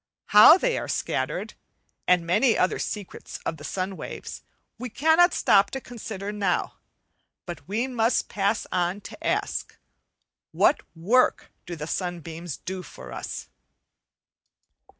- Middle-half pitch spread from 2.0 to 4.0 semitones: No, average, 4.9 semitones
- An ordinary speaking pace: No, slow, 130 wpm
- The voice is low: No, high, 195 Hz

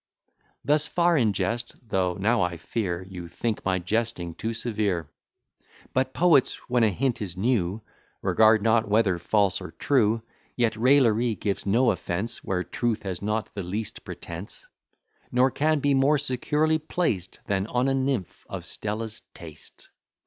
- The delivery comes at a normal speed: Yes, average, 155 wpm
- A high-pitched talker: No, low, 110 Hz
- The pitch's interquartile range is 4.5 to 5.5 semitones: Yes, average, 4.9 semitones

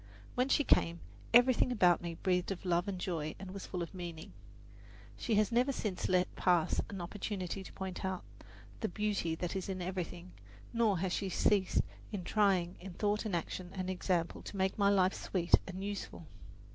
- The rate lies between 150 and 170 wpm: No, average, 185 wpm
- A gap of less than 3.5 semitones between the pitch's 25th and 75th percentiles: Yes, narrow, 2.5 semitones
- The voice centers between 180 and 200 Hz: Yes, medium, 185 Hz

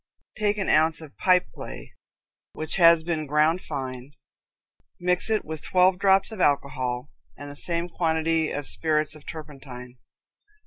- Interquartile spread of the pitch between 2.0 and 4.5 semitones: Yes, average, 3.7 semitones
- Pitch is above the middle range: No, medium, 160 Hz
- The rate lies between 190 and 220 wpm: No, average, 145 wpm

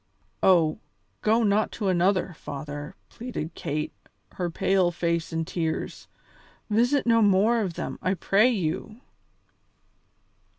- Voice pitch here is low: No, medium, 185 Hz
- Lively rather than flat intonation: No, average, 4.6 semitones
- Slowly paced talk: Yes, slow, 120 wpm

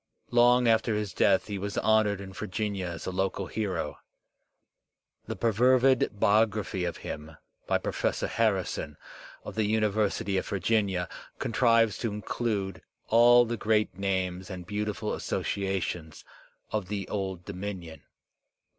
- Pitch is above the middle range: No, low, 100 Hz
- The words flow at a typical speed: No, slow, 130 wpm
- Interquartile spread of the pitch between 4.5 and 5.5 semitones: No, average, 2.8 semitones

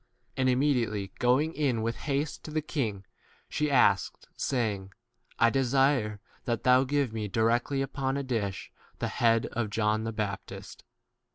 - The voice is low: Yes, low, 120 Hz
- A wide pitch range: No, average, 4.0 semitones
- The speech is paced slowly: No, average, 155 wpm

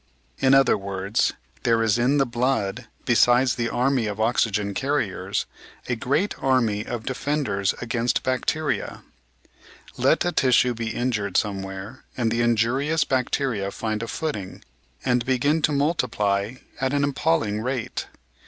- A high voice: No, low, 120 Hz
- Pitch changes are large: No, average, 3.9 semitones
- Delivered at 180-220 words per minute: No, slow, 135 wpm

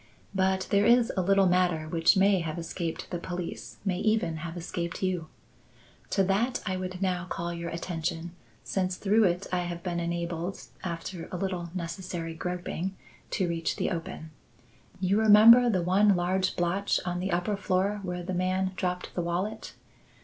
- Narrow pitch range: Yes, narrow, 2.0 semitones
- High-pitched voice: No, medium, 180 Hz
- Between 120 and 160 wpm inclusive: No, average, 170 wpm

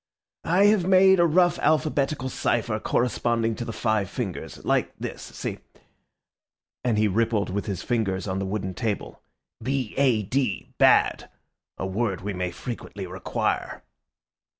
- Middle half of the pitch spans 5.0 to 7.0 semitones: Yes, average, 5.3 semitones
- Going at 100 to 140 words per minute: Yes, slow, 135 wpm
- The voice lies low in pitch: Yes, low, 115 Hz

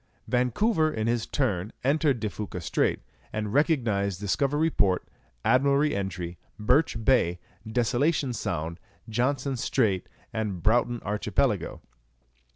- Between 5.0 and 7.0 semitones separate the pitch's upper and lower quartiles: Yes, wide, 5.5 semitones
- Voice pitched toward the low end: Yes, low, 115 Hz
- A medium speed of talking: No, slow, 110 wpm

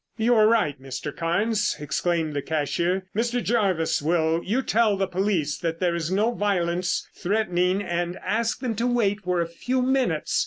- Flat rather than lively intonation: No, average, 4.8 semitones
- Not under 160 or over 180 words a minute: Yes, average, 170 wpm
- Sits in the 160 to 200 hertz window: Yes, medium, 185 Hz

